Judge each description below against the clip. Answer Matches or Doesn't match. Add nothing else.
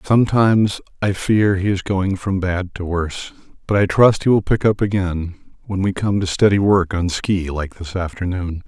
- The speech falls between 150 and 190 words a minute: Doesn't match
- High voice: Doesn't match